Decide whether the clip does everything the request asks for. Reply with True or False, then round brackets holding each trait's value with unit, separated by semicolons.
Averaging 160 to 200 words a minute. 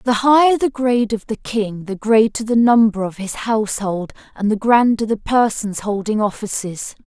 True (180 wpm)